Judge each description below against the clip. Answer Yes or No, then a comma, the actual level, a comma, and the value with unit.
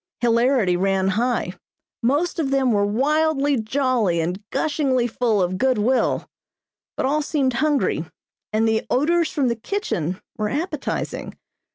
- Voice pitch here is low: No, very high, 250 Hz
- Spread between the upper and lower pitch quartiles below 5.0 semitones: No, average, 5.3 semitones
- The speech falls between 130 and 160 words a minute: Yes, average, 140 wpm